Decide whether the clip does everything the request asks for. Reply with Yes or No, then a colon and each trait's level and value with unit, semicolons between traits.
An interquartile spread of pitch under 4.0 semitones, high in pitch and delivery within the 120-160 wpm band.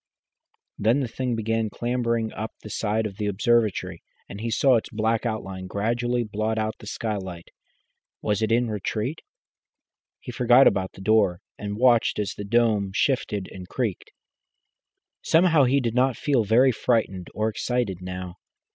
No: average, 3.0 semitones; low, 110 Hz; average, 155 wpm